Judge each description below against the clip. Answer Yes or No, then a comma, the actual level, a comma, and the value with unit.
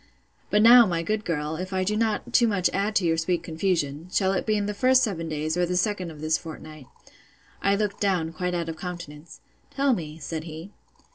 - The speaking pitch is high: No, medium, 180 Hz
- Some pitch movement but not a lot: Yes, average, 4.2 semitones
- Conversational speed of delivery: No, fast, 220 wpm